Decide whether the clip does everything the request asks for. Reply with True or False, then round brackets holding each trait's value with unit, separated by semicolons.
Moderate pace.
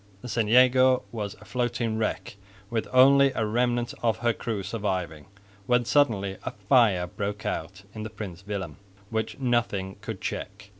True (160 wpm)